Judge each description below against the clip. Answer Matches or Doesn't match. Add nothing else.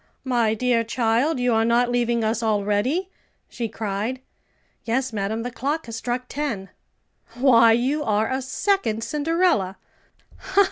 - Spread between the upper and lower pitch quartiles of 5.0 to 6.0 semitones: Doesn't match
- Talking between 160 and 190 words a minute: Doesn't match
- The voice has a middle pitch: Doesn't match